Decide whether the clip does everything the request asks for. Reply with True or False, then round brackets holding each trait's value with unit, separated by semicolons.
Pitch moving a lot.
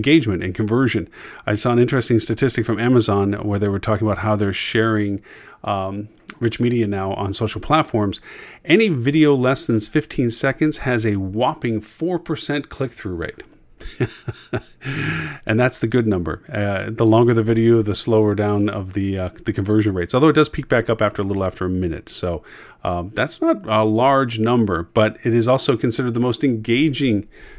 False (3.5 semitones)